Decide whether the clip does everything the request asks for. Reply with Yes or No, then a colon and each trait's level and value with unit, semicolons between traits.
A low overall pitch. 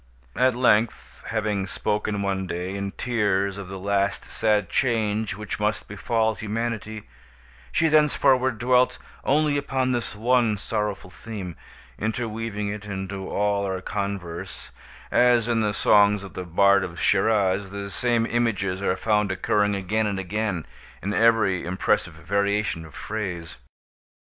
Yes: low, 105 Hz